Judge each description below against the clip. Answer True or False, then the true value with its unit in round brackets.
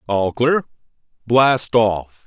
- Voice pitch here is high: False (115 Hz)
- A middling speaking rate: False (105 wpm)